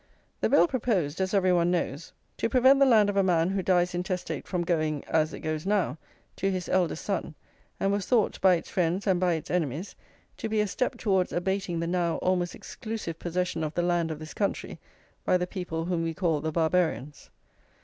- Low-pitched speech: No, medium, 180 Hz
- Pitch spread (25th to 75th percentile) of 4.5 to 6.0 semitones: No, average, 3.0 semitones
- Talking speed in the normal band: No, fast, 210 wpm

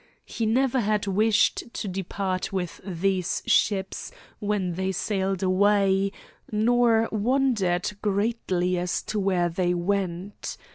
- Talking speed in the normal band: No, slow, 115 wpm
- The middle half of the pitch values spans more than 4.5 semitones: No, narrow, 2.5 semitones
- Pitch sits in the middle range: No, high, 195 Hz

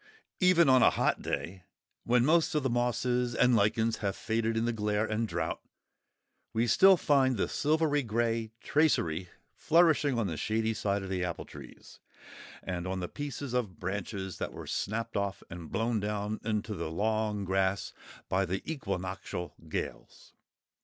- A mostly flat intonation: No, average, 4.3 semitones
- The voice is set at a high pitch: No, low, 110 Hz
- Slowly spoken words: No, average, 160 wpm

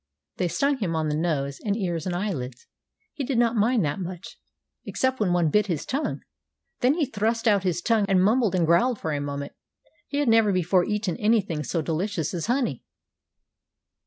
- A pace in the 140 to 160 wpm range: No, average, 190 wpm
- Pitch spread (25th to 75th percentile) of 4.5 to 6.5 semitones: Yes, wide, 5.6 semitones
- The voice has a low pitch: No, high, 190 Hz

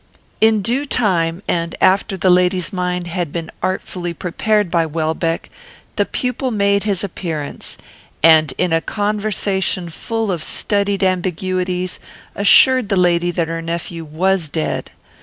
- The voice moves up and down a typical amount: Yes, average, 3.2 semitones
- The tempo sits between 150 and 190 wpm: No, average, 140 wpm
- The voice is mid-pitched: Yes, medium, 180 Hz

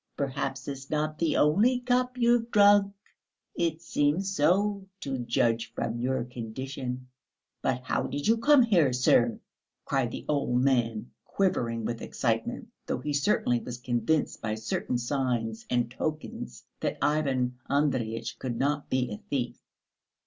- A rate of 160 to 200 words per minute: No, average, 140 wpm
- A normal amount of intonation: Yes, average, 4.7 semitones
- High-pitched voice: No, low, 135 Hz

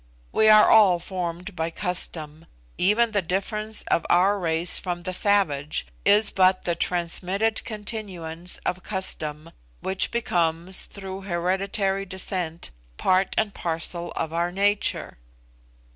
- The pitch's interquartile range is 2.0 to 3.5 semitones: Yes, average, 2.9 semitones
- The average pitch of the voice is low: No, medium, 185 Hz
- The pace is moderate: No, slow, 125 wpm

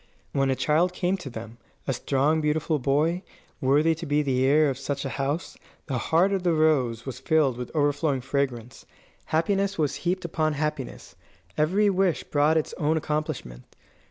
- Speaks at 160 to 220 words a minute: Yes, average, 170 wpm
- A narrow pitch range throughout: No, average, 3.2 semitones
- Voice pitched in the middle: Yes, medium, 150 Hz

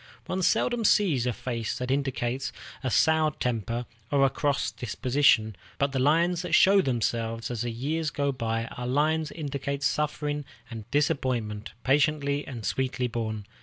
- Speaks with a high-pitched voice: No, low, 135 Hz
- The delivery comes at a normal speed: Yes, average, 160 wpm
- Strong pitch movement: No, average, 3.9 semitones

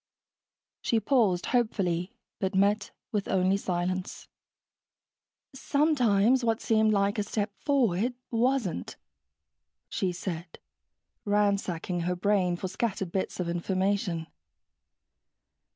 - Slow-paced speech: Yes, slow, 100 wpm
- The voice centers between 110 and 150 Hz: No, high, 200 Hz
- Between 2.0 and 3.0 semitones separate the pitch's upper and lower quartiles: No, average, 3.7 semitones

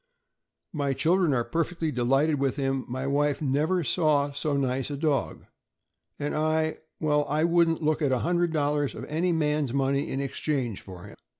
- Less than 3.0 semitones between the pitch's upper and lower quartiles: Yes, narrow, 2.6 semitones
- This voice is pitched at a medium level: Yes, medium, 145 Hz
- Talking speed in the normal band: Yes, average, 170 wpm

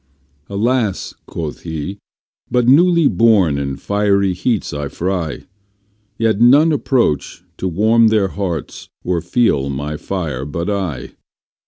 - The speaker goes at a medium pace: No, slow, 125 wpm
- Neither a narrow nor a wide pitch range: No, wide, 6.2 semitones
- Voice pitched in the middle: No, low, 100 Hz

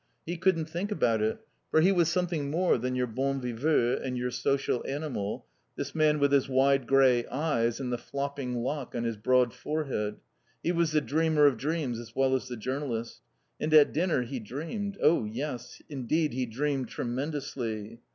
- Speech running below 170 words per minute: No, average, 180 wpm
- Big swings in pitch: No, average, 4.0 semitones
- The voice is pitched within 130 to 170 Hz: Yes, low, 135 Hz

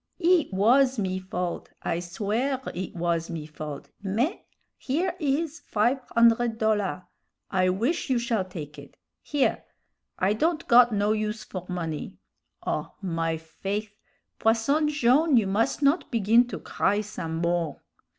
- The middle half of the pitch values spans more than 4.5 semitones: Yes, wide, 5.6 semitones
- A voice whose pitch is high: Yes, high, 210 Hz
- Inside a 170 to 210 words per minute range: No, average, 140 wpm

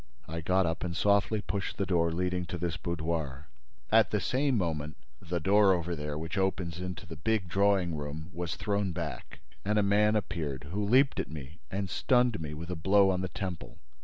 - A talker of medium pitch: No, very low, 90 Hz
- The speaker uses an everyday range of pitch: Yes, average, 3.6 semitones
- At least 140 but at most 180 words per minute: No, average, 200 wpm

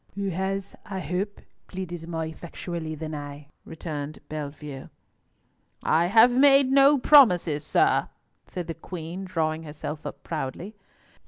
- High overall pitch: No, medium, 170 Hz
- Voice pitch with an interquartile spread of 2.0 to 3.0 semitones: No, average, 3.8 semitones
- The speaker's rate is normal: No, slow, 130 wpm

